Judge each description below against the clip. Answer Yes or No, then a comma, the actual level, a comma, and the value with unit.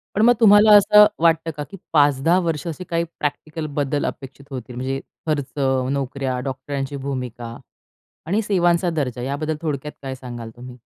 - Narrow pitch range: No, average, 4.1 semitones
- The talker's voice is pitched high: No, medium, 145 Hz